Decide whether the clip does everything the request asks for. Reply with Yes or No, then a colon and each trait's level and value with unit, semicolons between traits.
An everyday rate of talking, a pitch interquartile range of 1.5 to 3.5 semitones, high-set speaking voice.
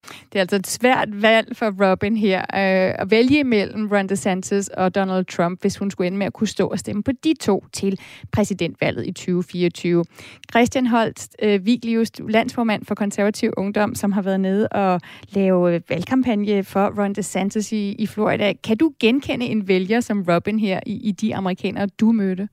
Yes: average, 175 wpm; average, 2.7 semitones; high, 200 Hz